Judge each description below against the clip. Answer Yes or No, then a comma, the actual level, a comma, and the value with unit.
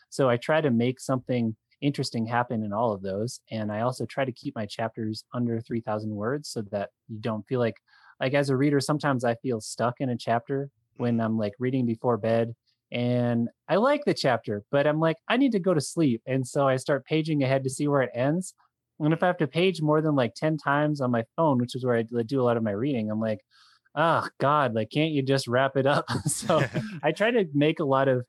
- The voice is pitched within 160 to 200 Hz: No, low, 130 Hz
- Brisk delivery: Yes, fast, 240 wpm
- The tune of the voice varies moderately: Yes, average, 4.1 semitones